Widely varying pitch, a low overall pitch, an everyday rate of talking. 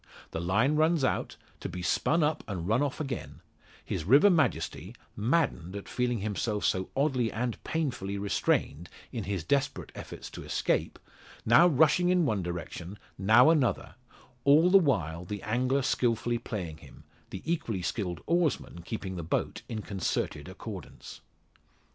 Yes: wide, 7.2 semitones; low, 115 Hz; average, 150 wpm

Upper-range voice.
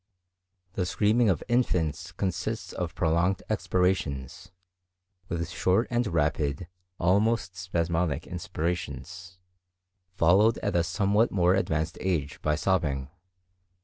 No: very low, 90 Hz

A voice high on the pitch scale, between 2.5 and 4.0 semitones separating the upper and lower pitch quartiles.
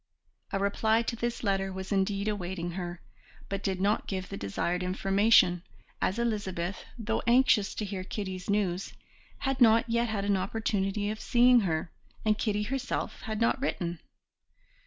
Yes: high, 200 Hz; average, 2.9 semitones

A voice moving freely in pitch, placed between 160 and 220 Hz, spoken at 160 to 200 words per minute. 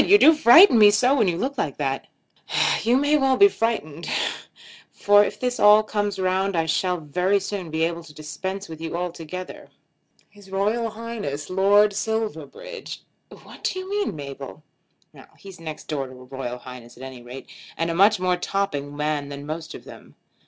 Yes: wide, 5.8 semitones; medium, 185 Hz; average, 185 wpm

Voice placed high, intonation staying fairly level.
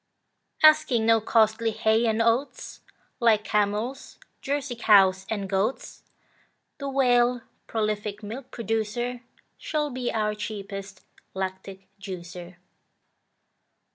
No: high, 220 Hz; average, 3.2 semitones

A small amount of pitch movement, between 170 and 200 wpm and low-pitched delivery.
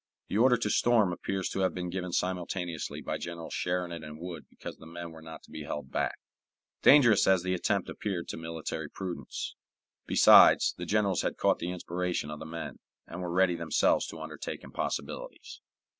Yes: narrow, 2.3 semitones; average, 185 wpm; very low, 90 Hz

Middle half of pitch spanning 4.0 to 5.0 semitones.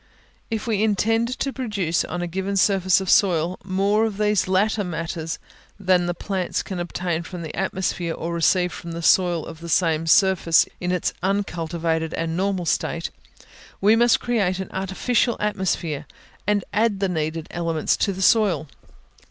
No: average, 3.2 semitones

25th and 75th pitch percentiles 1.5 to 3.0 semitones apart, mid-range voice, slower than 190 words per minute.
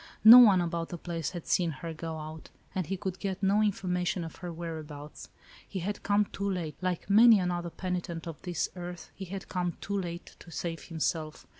No: narrow, 2.6 semitones; medium, 175 Hz; average, 200 wpm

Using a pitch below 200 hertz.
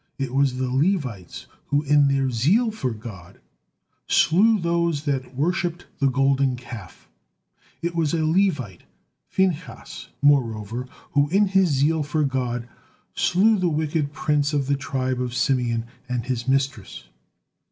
Yes: medium, 140 Hz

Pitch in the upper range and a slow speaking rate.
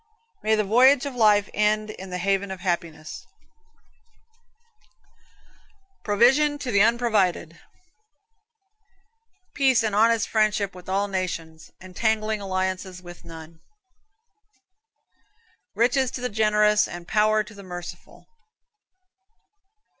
Yes: high, 210 Hz; slow, 105 wpm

